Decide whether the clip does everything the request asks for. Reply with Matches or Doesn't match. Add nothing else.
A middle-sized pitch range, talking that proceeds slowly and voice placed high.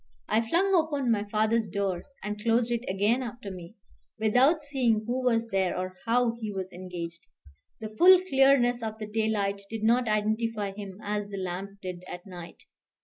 Doesn't match